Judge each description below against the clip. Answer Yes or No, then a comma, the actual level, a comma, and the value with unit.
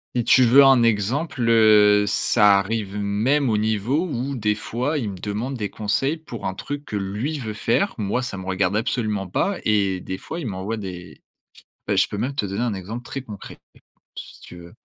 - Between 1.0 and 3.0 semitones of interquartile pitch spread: No, average, 4.1 semitones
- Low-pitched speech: Yes, low, 110 Hz